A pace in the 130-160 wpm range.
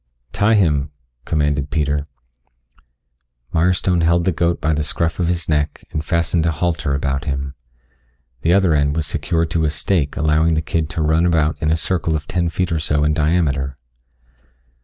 No: average, 180 wpm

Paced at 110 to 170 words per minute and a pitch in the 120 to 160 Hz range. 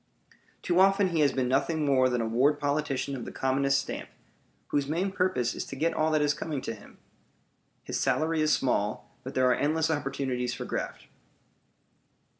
No: average, 185 wpm; medium, 140 Hz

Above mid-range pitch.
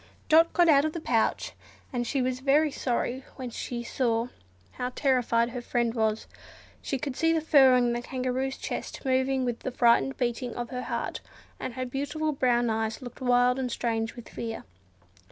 Yes: very high, 250 Hz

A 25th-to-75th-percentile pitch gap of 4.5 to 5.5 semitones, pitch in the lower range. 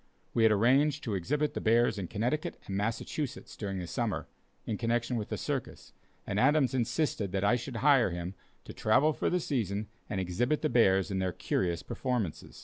Yes: average, 5.2 semitones; low, 115 Hz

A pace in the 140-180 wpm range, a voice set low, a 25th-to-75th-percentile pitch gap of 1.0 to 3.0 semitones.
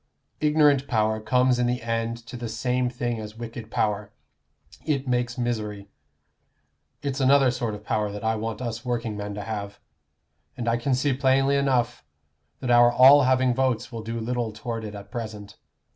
Yes: average, 175 wpm; low, 120 Hz; average, 2.7 semitones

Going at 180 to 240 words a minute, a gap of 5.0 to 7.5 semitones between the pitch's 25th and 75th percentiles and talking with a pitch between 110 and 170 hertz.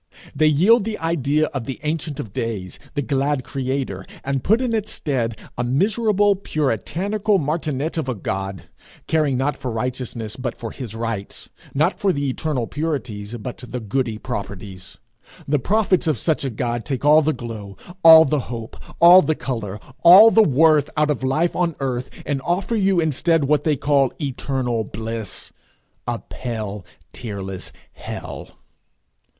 No: average, 160 wpm; wide, 5.5 semitones; low, 135 Hz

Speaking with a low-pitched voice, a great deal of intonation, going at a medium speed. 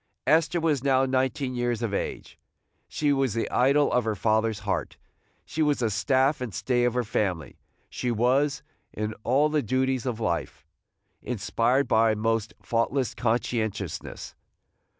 No: low, 125 Hz; average, 3.4 semitones; average, 150 wpm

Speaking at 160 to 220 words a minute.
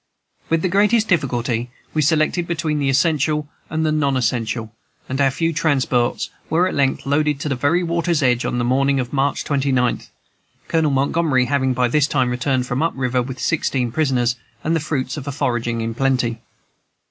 Yes: average, 180 wpm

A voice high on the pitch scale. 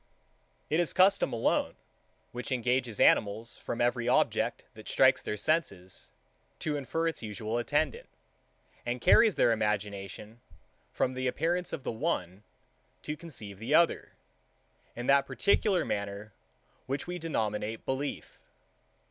No: low, 120 Hz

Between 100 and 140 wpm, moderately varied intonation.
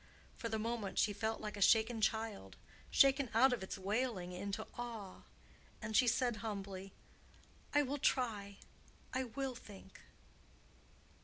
Yes: slow, 135 wpm; average, 3.4 semitones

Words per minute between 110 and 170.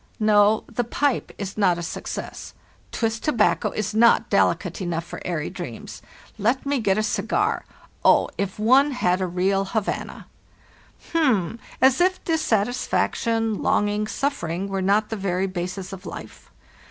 Yes: average, 145 wpm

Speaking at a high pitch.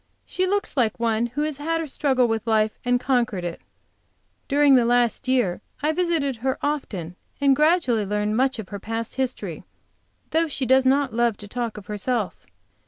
Yes: high, 245 Hz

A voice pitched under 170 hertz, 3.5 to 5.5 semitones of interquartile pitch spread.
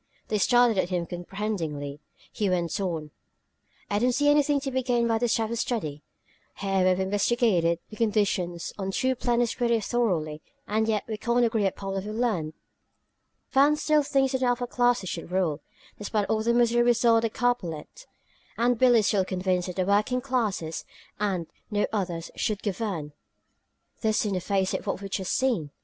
No: high, 210 Hz; average, 4.7 semitones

